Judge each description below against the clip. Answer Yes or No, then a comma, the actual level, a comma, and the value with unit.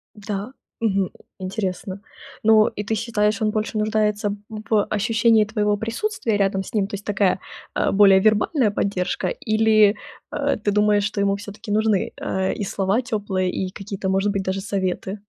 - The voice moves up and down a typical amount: No, narrow, 1.7 semitones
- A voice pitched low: No, high, 205 Hz